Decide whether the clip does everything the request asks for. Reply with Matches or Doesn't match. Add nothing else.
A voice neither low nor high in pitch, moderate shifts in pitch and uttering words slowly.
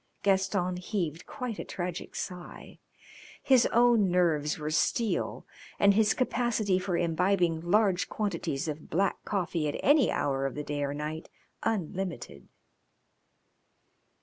Matches